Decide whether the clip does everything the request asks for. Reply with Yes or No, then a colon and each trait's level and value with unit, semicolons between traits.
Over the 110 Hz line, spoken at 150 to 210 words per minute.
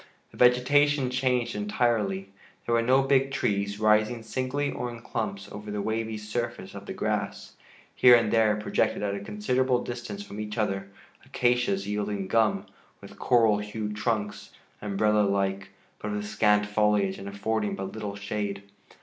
No: low, 105 Hz; average, 160 wpm